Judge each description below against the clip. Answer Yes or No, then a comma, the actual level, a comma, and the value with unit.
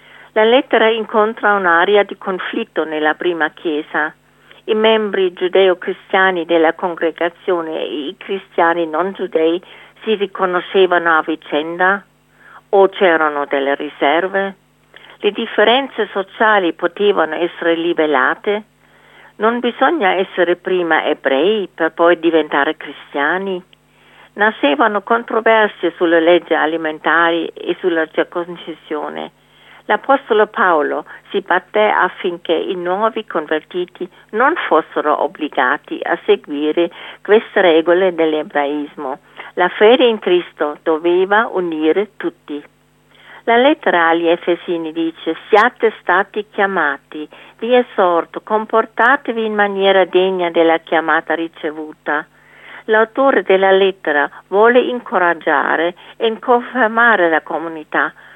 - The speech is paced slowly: Yes, slow, 100 wpm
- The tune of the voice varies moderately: Yes, average, 4.8 semitones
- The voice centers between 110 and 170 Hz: No, medium, 180 Hz